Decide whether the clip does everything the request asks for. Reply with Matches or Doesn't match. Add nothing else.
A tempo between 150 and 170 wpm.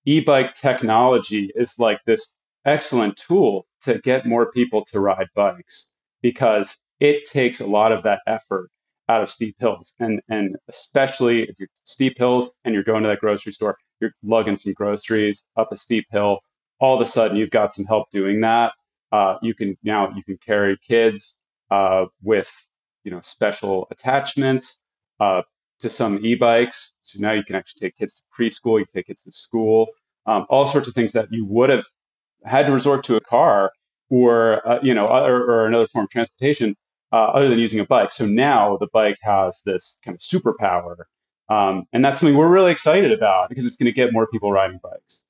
Doesn't match